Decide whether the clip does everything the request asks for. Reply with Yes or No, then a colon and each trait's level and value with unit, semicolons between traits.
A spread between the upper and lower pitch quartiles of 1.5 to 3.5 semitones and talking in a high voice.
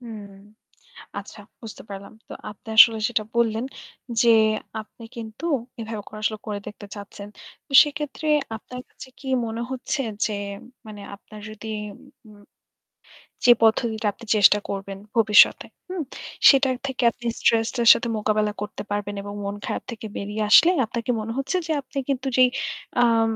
Yes: average, 2.9 semitones; high, 225 Hz